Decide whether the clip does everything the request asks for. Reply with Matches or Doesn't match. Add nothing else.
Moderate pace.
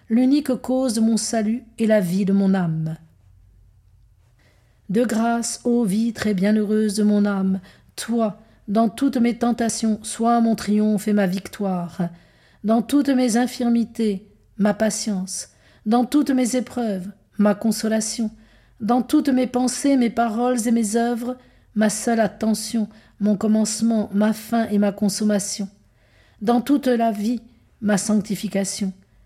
Doesn't match